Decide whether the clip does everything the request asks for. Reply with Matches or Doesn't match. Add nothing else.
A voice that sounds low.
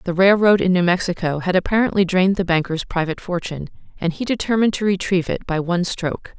Doesn't match